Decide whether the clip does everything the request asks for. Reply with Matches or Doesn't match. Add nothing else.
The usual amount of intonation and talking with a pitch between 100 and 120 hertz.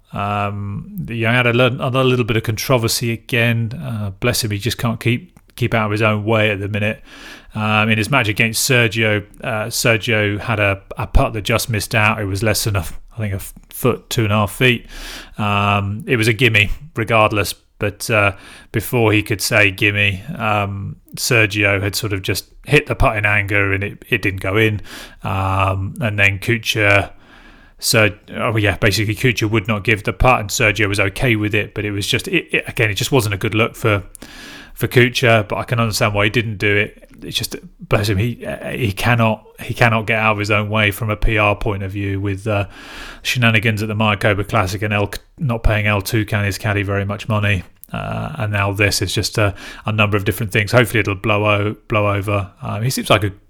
Doesn't match